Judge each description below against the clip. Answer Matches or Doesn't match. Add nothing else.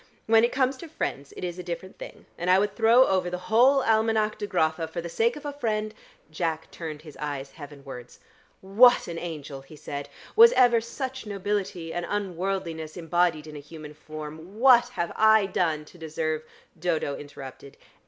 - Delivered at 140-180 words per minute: Doesn't match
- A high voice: Doesn't match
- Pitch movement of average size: Doesn't match